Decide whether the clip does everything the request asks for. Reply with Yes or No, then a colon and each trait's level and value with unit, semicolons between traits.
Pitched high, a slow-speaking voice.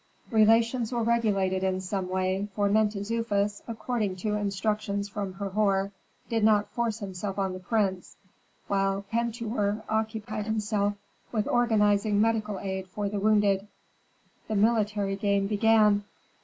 Yes: high, 205 Hz; slow, 130 wpm